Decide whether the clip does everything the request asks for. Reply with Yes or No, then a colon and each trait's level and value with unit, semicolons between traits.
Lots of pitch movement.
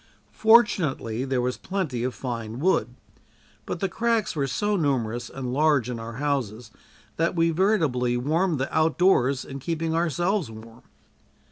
Yes: wide, 5.8 semitones